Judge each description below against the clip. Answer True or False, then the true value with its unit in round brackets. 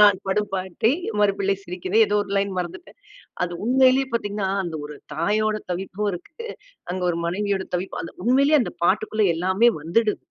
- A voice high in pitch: True (200 Hz)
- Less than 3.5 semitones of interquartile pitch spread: True (2.8 semitones)